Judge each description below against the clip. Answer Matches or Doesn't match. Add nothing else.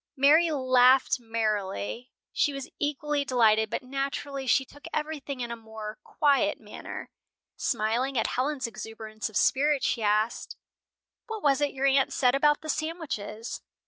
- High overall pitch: Matches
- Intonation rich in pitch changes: Doesn't match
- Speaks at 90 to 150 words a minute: Matches